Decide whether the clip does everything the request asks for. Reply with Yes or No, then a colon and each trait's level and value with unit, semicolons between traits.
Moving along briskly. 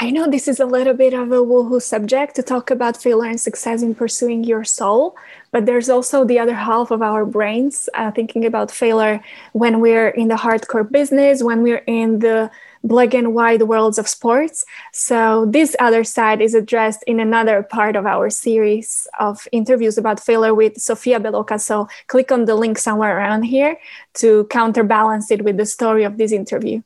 No: average, 190 wpm